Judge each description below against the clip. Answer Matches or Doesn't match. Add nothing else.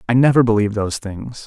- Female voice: Doesn't match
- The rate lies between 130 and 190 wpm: Doesn't match